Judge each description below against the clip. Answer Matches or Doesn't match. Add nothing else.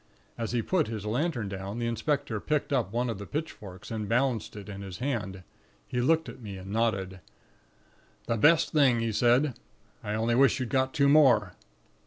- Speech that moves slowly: Doesn't match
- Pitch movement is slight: Doesn't match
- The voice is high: Doesn't match